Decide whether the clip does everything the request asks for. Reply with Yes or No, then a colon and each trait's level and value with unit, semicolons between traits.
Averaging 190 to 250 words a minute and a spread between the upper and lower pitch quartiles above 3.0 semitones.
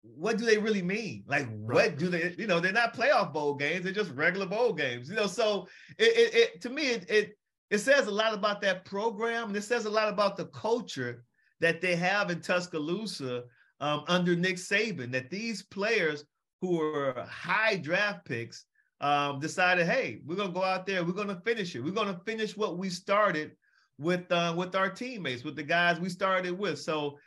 Yes: fast, 205 wpm; average, 4.9 semitones